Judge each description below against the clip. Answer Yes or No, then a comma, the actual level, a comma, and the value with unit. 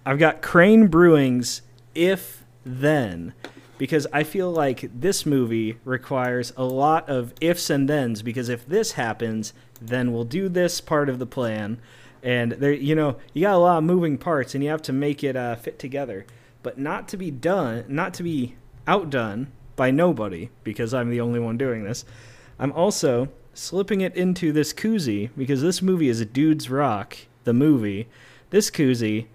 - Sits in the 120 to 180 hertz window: Yes, low, 135 Hz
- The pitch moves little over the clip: No, average, 4.6 semitones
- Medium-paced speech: Yes, average, 180 wpm